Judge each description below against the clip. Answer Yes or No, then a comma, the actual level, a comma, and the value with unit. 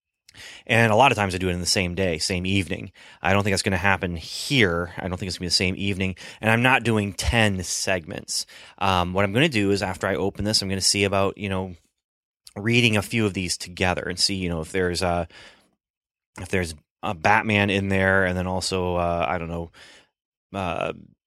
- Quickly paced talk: Yes, fast, 225 wpm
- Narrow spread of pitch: Yes, narrow, 2.1 semitones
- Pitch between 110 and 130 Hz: No, very low, 95 Hz